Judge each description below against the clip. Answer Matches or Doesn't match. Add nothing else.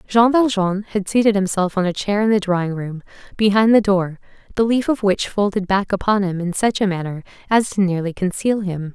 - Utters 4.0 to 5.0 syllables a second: Doesn't match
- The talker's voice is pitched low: Doesn't match